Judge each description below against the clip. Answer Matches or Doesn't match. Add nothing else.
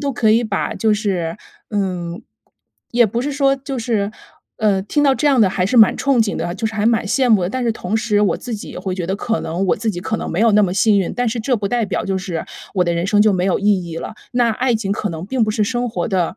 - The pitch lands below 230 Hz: Matches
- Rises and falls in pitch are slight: Doesn't match